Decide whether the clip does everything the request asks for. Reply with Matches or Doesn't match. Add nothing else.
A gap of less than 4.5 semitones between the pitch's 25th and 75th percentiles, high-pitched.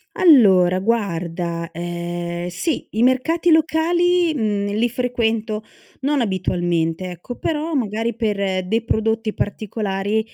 Doesn't match